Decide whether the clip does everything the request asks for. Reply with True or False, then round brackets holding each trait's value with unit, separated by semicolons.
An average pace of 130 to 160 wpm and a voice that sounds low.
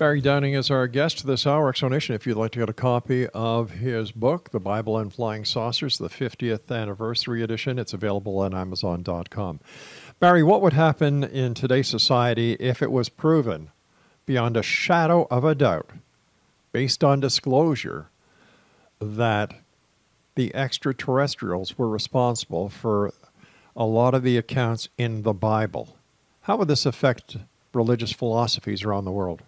True (150 wpm; 120 Hz)